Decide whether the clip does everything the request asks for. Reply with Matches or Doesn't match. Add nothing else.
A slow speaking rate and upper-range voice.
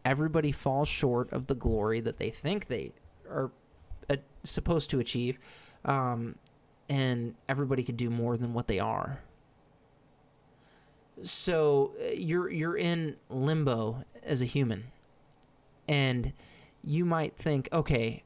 Doesn't match